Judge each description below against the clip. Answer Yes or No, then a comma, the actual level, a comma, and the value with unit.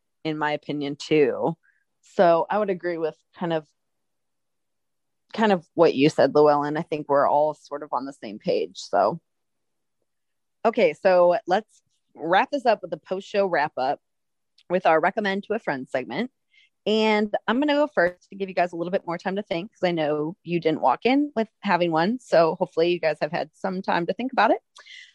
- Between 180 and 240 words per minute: Yes, average, 200 wpm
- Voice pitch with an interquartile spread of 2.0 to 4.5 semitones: No, average, 5.0 semitones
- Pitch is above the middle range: No, medium, 175 Hz